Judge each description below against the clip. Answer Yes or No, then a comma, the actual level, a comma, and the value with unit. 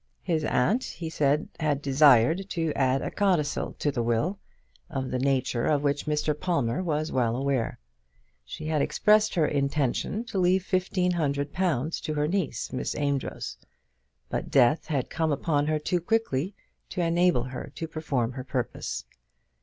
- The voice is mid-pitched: Yes, medium, 150 Hz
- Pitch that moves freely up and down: No, average, 4.2 semitones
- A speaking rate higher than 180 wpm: No, average, 160 wpm